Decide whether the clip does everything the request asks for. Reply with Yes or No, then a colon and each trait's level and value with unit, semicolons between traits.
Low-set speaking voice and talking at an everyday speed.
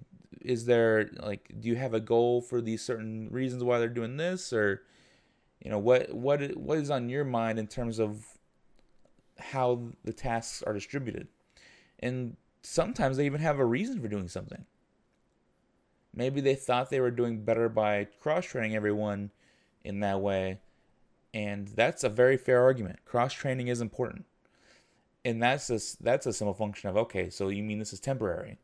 Yes: low, 115 Hz; average, 170 wpm